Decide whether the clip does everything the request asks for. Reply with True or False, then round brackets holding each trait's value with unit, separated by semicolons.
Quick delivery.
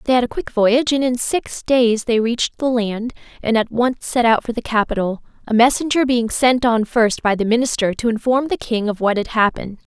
True (230 wpm)